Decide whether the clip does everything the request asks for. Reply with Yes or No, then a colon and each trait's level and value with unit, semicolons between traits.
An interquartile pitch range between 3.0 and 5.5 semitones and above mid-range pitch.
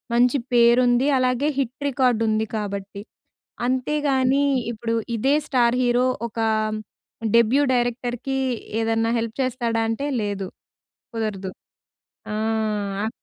No: narrow, 2.4 semitones; high, 240 Hz